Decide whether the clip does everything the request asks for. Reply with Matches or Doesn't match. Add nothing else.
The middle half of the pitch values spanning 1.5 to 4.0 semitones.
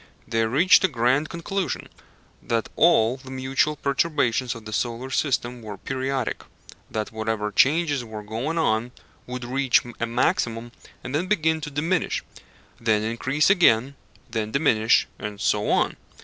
Doesn't match